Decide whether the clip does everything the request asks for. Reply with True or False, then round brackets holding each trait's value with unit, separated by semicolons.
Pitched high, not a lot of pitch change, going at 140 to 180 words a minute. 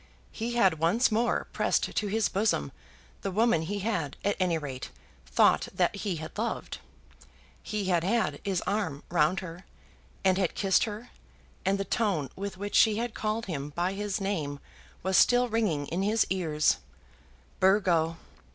False (195 Hz; 4.3 semitones; 160 wpm)